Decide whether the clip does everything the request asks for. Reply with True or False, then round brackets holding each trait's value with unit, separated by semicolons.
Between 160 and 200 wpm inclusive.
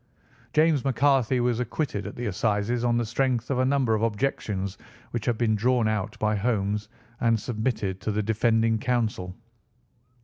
True (170 wpm)